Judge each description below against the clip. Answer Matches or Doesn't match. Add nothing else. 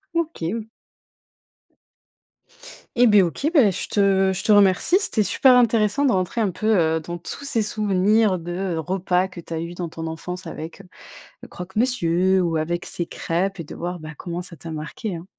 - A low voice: Doesn't match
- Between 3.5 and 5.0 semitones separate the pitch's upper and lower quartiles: Matches